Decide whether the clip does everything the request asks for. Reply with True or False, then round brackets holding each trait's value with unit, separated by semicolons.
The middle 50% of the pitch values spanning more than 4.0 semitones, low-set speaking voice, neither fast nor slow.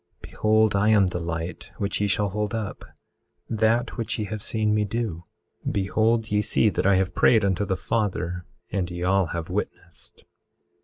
False (2.8 semitones; 105 Hz; 170 wpm)